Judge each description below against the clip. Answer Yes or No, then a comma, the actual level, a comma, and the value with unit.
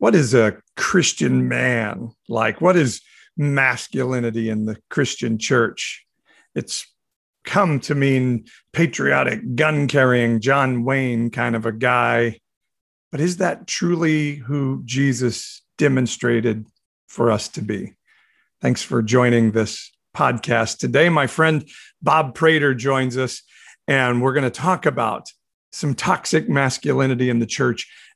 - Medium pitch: No, low, 130 Hz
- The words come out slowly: Yes, slow, 130 wpm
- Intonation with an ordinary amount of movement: Yes, average, 3.7 semitones